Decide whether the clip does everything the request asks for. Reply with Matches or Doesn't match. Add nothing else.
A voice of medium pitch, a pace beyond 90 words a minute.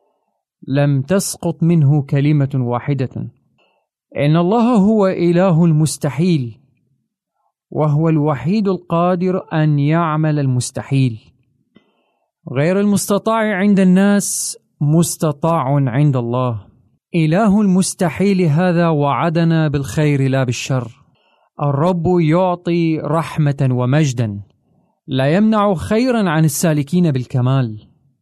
Doesn't match